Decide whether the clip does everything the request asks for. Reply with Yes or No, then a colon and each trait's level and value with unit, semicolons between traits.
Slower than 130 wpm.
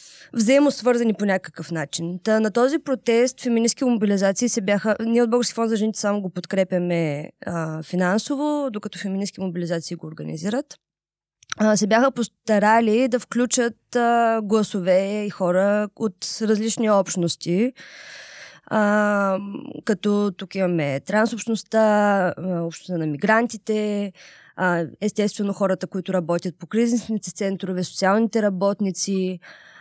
Yes: average, 120 wpm